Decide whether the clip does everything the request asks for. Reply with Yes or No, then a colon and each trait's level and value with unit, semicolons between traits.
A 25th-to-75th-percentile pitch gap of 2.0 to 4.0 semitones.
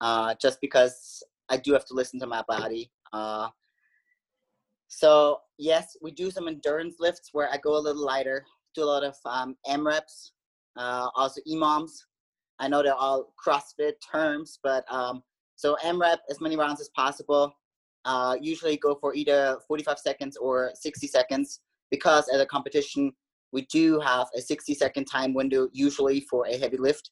Yes: average, 3.0 semitones